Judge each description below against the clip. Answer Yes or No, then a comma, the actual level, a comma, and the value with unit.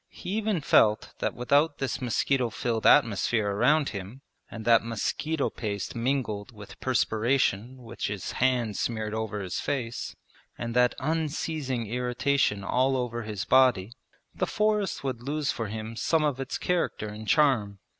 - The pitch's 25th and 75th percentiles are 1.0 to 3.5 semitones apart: No, average, 4.1 semitones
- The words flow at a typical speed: Yes, average, 150 wpm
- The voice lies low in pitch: Yes, low, 120 Hz